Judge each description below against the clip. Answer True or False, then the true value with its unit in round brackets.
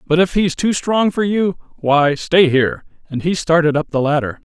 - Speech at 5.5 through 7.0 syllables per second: False (4.9 syllables/s)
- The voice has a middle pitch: True (165 Hz)